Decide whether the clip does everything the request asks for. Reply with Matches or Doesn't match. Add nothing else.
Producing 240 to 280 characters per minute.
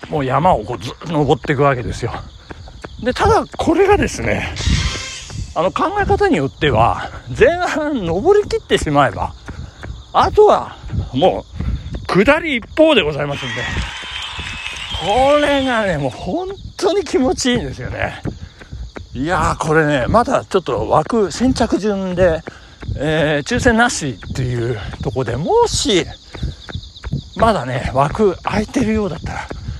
Matches